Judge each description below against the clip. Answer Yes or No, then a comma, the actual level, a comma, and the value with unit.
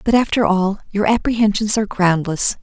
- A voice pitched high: Yes, high, 205 Hz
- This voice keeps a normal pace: Yes, average, 160 wpm